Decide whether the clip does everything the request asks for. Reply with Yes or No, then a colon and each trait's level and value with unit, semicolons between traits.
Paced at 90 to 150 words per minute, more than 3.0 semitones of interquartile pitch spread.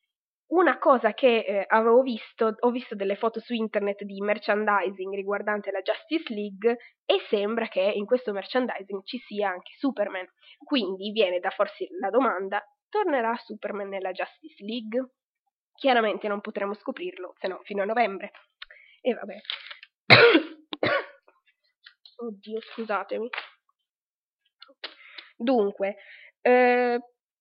Yes: average, 120 wpm; average, 4.2 semitones